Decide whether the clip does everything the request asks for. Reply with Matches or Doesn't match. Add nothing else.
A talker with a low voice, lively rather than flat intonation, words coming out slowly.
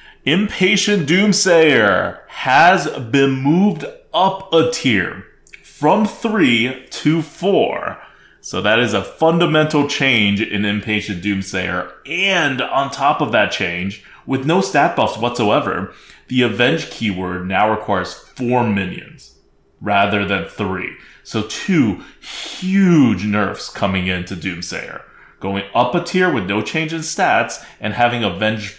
Matches